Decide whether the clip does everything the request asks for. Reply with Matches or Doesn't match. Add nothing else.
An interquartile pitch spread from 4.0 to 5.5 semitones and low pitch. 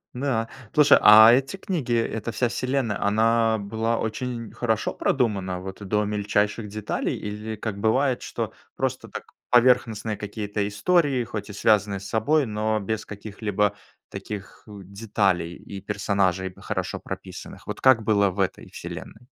Doesn't match